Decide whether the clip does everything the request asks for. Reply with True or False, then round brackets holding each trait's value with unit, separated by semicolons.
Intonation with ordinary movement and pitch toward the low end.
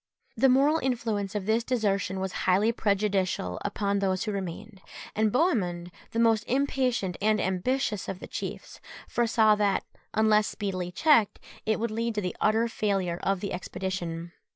False (3.3 semitones; 210 Hz)